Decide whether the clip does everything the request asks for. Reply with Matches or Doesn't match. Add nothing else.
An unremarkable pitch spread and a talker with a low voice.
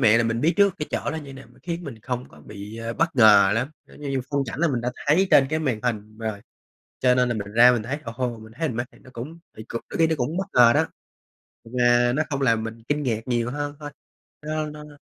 Matches